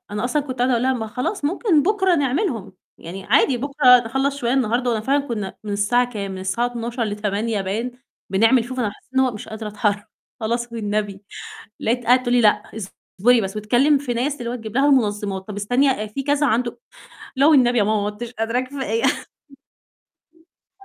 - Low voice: No, high, 240 Hz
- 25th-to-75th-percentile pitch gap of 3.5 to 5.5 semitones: Yes, average, 3.8 semitones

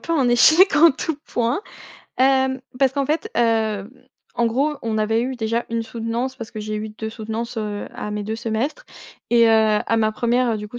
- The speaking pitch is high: Yes, high, 230 Hz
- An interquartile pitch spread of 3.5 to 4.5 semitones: No, average, 3.1 semitones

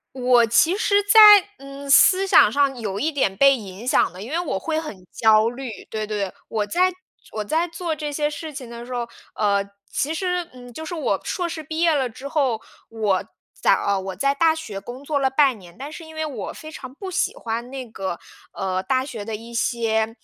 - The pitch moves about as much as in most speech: No, wide, 6.1 semitones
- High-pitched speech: Yes, very high, 260 Hz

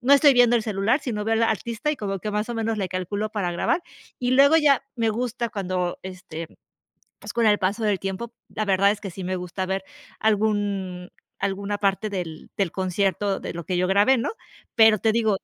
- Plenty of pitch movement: No, average, 3.2 semitones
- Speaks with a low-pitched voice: No, high, 205 Hz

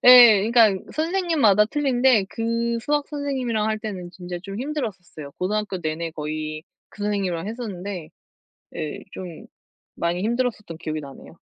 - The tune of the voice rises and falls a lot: Yes, wide, 5.7 semitones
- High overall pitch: Yes, high, 210 Hz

